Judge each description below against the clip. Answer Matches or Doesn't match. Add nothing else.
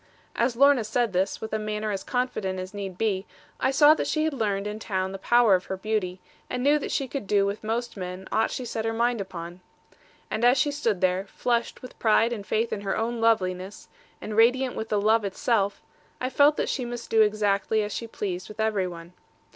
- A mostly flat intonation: Doesn't match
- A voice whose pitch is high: Matches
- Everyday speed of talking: Doesn't match